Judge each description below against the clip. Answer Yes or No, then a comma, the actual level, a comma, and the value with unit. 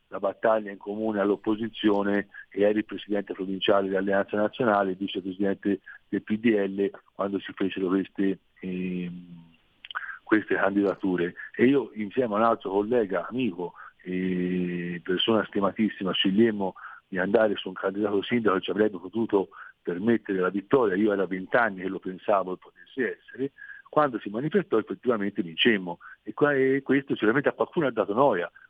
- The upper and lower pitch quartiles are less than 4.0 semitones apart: Yes, narrow, 2.5 semitones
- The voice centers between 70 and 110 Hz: Yes, low, 100 Hz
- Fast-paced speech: No, average, 145 wpm